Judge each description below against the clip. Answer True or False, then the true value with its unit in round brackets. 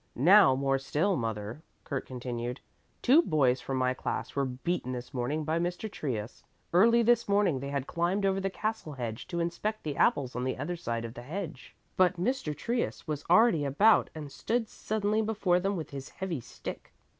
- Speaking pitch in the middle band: True (155 Hz)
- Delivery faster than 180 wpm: True (190 wpm)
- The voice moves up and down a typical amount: False (7.3 semitones)